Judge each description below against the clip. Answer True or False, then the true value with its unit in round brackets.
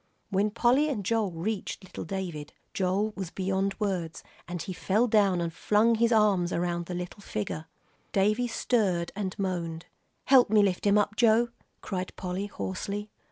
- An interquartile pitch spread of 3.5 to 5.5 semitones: False (3.0 semitones)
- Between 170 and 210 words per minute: False (160 wpm)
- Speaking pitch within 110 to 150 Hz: False (195 Hz)